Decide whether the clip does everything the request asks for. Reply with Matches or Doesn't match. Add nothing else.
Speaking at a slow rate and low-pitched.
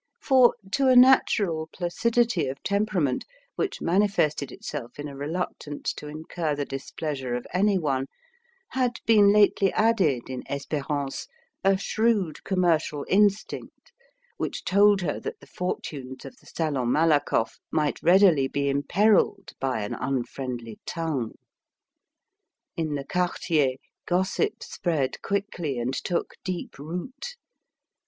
Doesn't match